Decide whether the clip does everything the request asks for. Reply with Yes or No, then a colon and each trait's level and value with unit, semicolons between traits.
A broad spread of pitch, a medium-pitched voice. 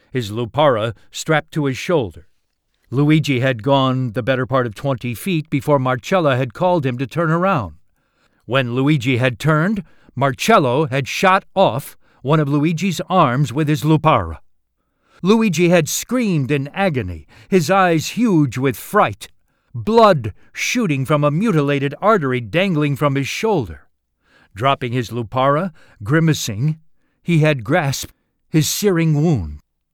No: average, 4.8 semitones; medium, 145 Hz